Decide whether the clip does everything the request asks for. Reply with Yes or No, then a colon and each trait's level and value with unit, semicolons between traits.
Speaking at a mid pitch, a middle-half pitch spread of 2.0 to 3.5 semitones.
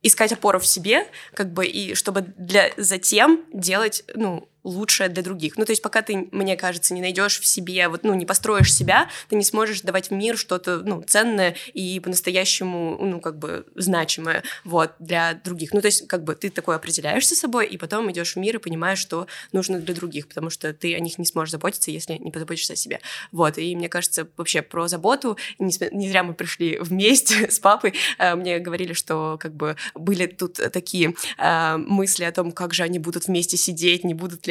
Yes: medium, 180 Hz; average, 2.7 semitones